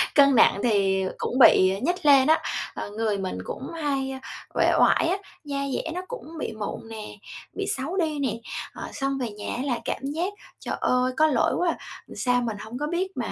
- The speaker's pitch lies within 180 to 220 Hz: No, very high, 270 Hz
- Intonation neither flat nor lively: No, wide, 5.8 semitones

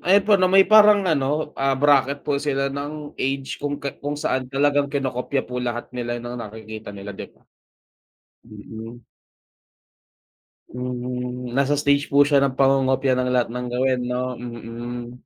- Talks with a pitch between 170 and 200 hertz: No, low, 130 Hz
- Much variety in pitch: No, narrow, 2.6 semitones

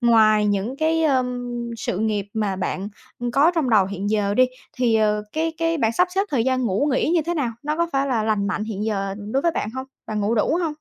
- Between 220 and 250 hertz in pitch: Yes, high, 230 Hz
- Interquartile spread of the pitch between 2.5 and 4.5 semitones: No, average, 5.0 semitones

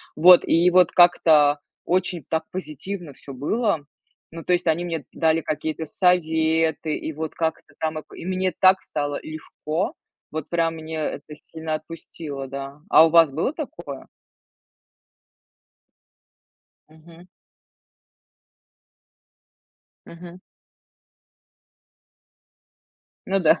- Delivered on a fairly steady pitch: Yes, narrow, 2.3 semitones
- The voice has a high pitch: No, medium, 160 Hz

